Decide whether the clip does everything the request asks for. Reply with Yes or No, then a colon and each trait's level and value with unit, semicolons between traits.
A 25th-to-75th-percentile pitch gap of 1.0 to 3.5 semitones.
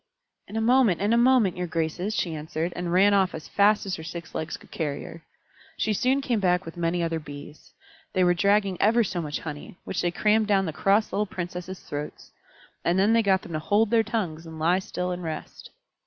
No: average, 4.0 semitones